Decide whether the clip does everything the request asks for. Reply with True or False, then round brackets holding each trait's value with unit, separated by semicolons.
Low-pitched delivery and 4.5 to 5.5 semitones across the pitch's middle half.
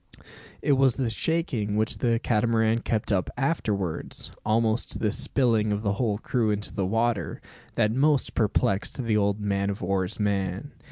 False (110 Hz; 2.8 semitones)